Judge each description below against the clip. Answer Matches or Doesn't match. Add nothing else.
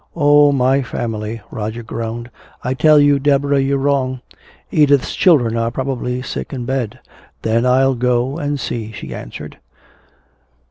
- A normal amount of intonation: Matches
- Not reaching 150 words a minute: Matches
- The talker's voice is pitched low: Matches